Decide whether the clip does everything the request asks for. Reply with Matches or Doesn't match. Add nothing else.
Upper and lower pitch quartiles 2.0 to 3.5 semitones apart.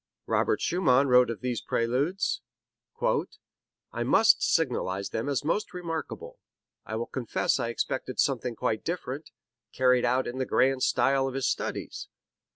Matches